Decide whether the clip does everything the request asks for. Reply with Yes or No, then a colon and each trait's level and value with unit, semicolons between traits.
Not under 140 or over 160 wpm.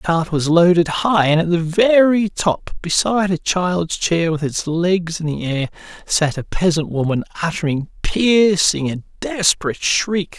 No: average, 170 wpm